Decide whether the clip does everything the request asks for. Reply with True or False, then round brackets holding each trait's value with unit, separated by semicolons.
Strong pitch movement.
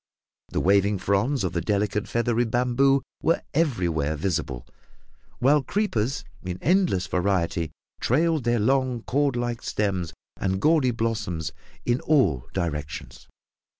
True (6.4 semitones)